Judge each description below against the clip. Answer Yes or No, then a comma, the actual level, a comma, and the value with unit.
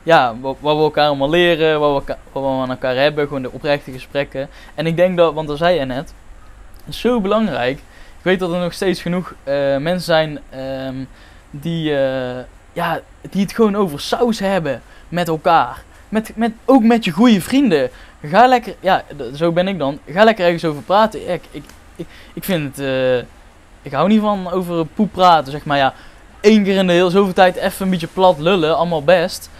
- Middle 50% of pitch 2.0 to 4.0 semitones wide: No, wide, 5.6 semitones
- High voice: No, medium, 165 Hz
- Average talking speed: No, fast, 205 wpm